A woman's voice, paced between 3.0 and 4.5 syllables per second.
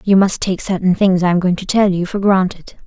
No: female; 5.6 syllables/s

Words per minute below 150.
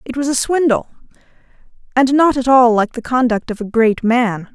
No: average, 200 wpm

